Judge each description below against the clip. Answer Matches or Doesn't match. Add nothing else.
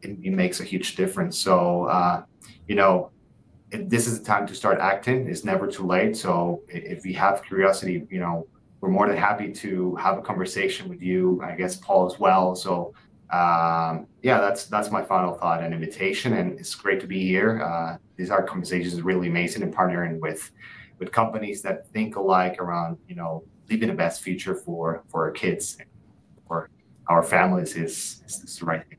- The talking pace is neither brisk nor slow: Matches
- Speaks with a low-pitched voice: Matches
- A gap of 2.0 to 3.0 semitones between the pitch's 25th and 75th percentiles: Matches